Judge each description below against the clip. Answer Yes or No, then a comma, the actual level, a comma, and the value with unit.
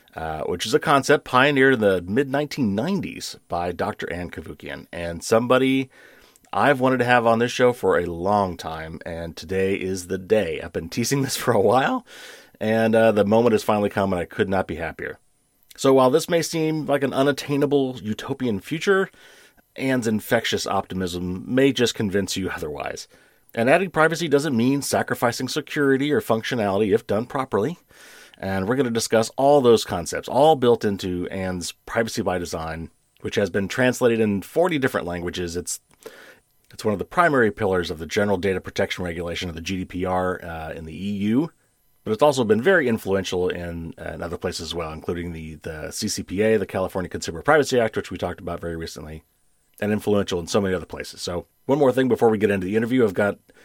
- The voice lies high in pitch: No, low, 110 Hz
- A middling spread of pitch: No, wide, 6.7 semitones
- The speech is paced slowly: No, average, 190 wpm